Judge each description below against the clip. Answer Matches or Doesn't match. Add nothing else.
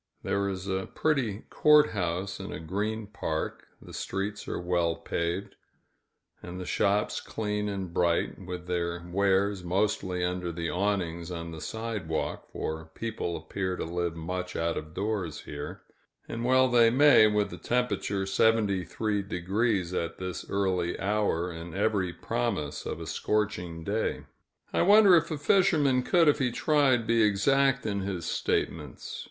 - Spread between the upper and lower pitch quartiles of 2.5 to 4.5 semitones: Matches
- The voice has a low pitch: Matches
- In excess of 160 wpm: Doesn't match